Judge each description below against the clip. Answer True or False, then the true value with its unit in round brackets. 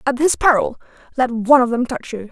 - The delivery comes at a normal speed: False (235 wpm)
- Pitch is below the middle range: False (250 Hz)